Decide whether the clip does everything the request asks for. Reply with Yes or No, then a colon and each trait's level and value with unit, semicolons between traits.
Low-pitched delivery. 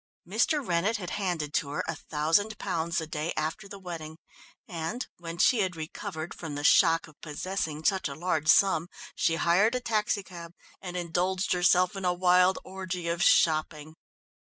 No: medium, 175 Hz